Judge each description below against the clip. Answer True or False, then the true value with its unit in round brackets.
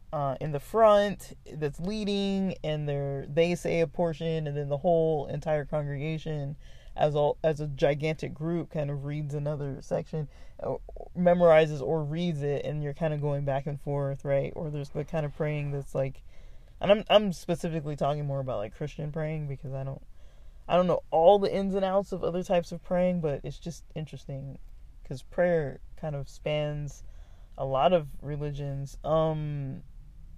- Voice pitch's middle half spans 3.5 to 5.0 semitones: False (2.9 semitones)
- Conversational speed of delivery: True (180 wpm)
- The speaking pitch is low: False (150 Hz)